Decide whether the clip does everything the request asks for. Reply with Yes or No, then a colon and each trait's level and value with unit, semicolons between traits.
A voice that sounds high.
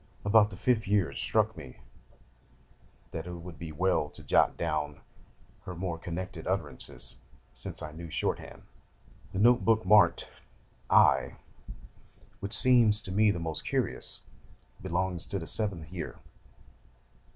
No: very low, 90 Hz